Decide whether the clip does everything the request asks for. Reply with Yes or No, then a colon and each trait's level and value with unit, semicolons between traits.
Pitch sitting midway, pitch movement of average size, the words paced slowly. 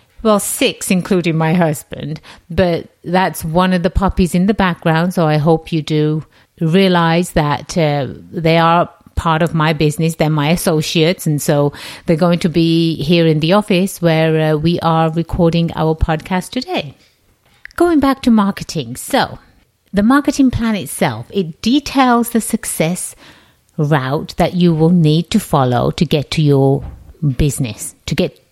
No: medium, 165 Hz; average, 3.2 semitones; average, 160 wpm